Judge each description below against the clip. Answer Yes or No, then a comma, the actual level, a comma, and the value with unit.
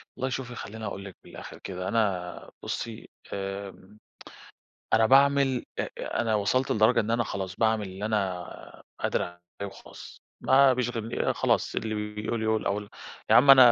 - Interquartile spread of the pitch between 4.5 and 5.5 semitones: No, average, 3.4 semitones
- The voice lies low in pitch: Yes, low, 110 Hz